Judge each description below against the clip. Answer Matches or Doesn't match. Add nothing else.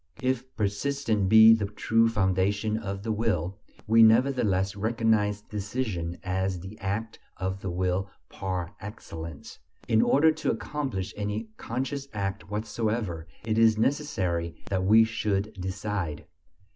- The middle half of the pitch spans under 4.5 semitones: Matches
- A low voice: Matches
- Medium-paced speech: Doesn't match